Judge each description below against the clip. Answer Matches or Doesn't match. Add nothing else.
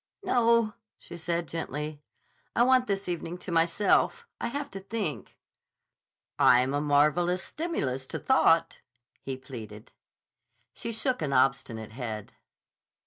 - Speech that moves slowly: Matches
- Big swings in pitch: Matches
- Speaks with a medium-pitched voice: Matches